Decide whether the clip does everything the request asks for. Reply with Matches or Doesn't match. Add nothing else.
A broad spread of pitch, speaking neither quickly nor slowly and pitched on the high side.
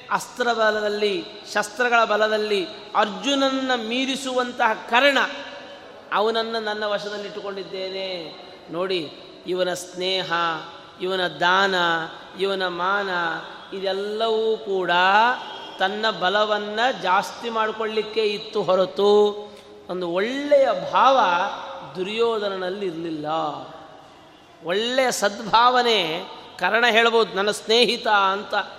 Doesn't match